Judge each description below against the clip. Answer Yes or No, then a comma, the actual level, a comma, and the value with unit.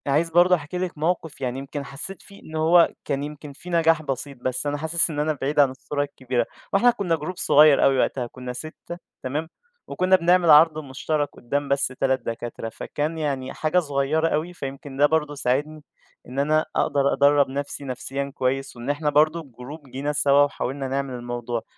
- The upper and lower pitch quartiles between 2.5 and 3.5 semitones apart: Yes, average, 2.8 semitones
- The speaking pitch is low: No, medium, 145 Hz